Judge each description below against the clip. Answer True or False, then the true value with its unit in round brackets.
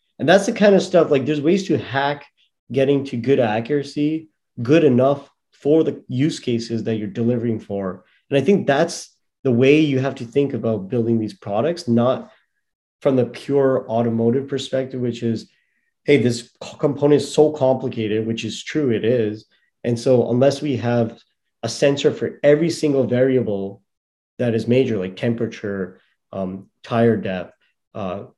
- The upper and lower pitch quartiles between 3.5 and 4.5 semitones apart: True (3.8 semitones)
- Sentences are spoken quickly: False (165 wpm)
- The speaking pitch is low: True (125 Hz)